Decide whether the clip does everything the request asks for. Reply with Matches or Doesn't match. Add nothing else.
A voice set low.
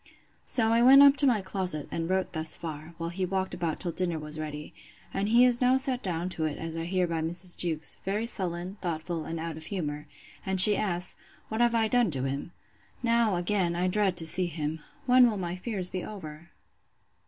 Doesn't match